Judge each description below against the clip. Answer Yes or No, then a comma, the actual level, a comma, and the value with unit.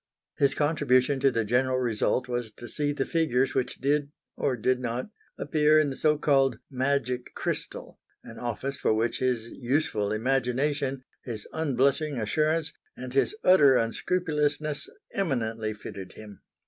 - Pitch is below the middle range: Yes, low, 130 Hz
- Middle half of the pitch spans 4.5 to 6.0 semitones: No, average, 3.5 semitones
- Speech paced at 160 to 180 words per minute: No, average, 145 wpm